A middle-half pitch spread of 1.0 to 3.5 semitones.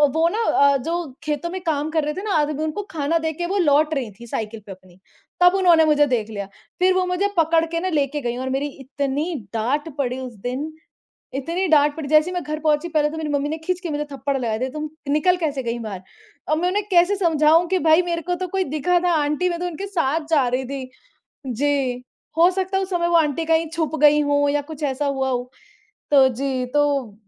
No: average, 3.9 semitones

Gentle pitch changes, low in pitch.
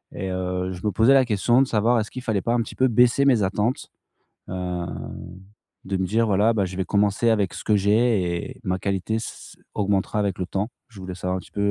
No: average, 3.6 semitones; low, 100 Hz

